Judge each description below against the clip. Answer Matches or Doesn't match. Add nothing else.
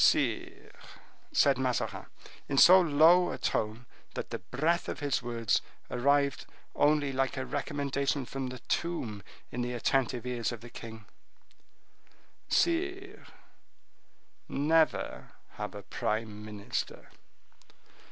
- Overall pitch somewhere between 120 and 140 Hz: Matches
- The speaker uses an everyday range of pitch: Matches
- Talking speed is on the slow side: Matches